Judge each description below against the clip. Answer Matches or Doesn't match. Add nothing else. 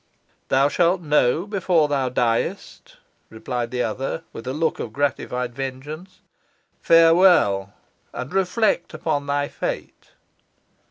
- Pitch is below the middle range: Doesn't match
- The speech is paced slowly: Matches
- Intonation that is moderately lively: Matches